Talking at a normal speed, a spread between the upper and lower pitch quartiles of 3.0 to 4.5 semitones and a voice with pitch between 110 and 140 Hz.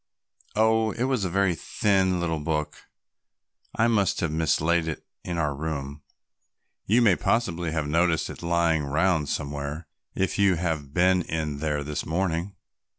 No: average, 150 wpm; average, 3.8 semitones; very low, 85 Hz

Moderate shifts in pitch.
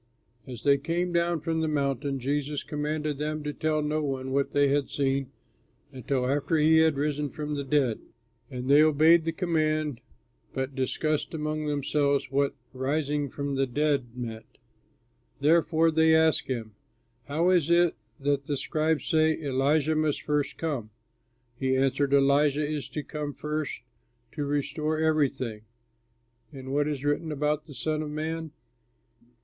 No: narrow, 2.1 semitones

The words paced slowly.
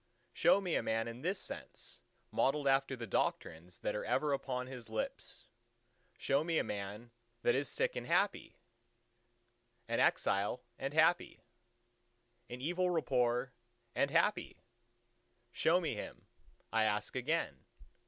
Yes: slow, 125 wpm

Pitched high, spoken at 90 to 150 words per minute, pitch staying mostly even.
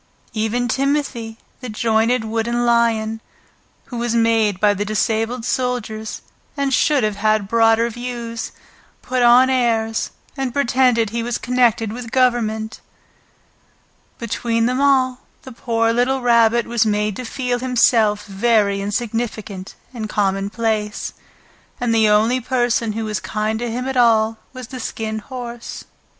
Yes: high, 230 Hz; slow, 135 wpm; narrow, 2.1 semitones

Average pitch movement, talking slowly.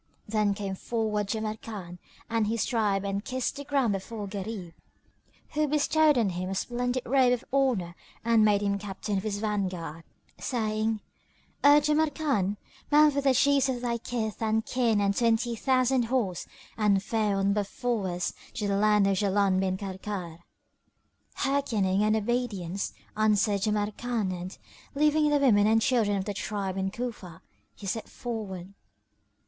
No: average, 3.7 semitones; average, 155 wpm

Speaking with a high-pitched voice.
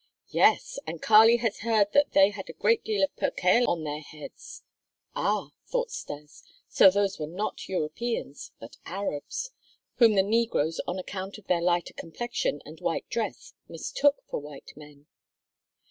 Yes: high, 195 Hz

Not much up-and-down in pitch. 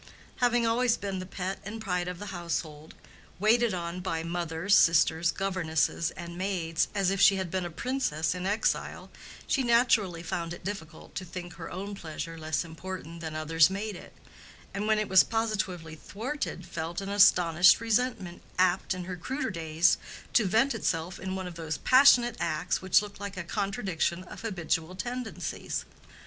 No: average, 3.6 semitones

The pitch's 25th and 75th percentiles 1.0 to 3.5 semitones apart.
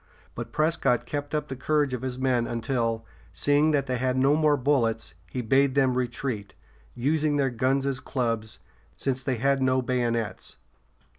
Yes: narrow, 2.6 semitones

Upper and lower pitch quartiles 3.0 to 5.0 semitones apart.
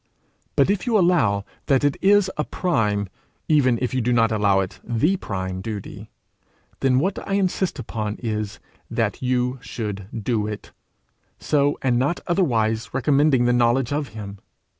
No: wide, 5.5 semitones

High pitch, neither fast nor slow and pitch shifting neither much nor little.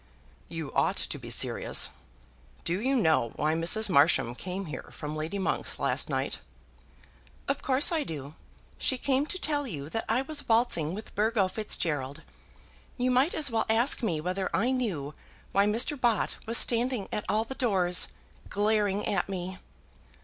No: high, 210 Hz; average, 165 wpm; wide, 6.8 semitones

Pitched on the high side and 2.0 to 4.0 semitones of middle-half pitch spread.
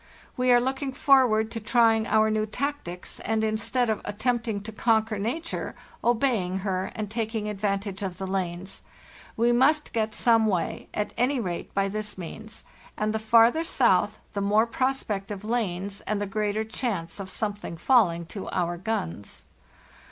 Yes: high, 215 Hz; average, 3.0 semitones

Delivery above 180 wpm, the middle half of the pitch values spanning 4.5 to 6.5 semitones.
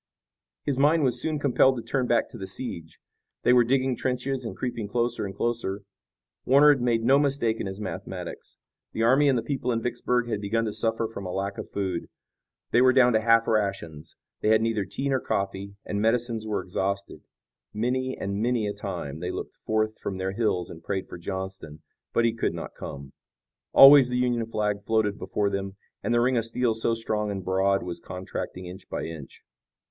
No: fast, 205 wpm; average, 3.9 semitones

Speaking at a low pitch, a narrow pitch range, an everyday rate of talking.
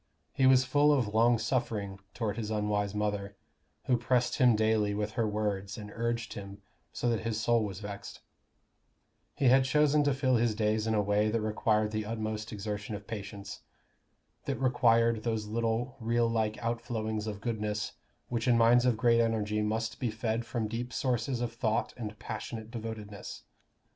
Yes: low, 110 Hz; narrow, 2.0 semitones; average, 175 wpm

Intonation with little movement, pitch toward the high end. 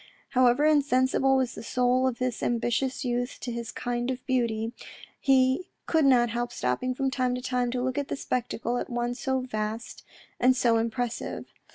Yes: narrow, 1.5 semitones; very high, 250 Hz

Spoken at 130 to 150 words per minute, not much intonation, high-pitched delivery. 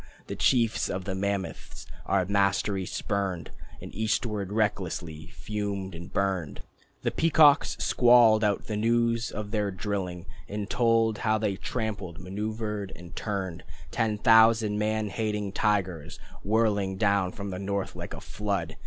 No: average, 140 wpm; narrow, 2.2 semitones; low, 105 Hz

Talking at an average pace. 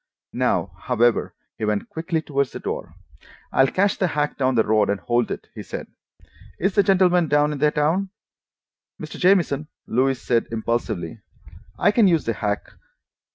Yes: average, 165 wpm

